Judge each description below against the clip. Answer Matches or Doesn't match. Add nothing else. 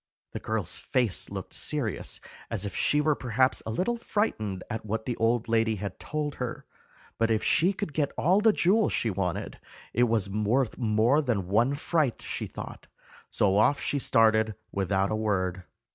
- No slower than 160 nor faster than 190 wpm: Matches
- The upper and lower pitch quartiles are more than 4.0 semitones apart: Matches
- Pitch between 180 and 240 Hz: Doesn't match